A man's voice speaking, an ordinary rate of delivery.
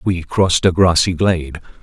Yes: male; average, 165 wpm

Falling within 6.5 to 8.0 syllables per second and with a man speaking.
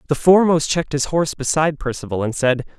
Yes: 6.8 syllables/s; male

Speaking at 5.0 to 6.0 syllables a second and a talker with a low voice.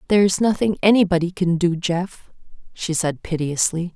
No: 5.2 syllables/s; medium, 180 Hz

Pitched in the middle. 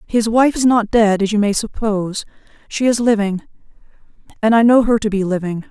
No: high, 215 Hz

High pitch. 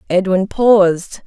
Yes: high, 195 Hz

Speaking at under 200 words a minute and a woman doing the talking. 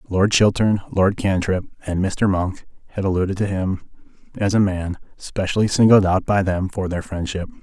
No: average, 175 wpm; male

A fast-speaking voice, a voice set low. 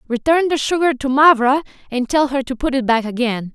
No: fast, 220 wpm; very high, 265 Hz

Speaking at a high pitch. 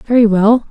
Yes: high, 220 Hz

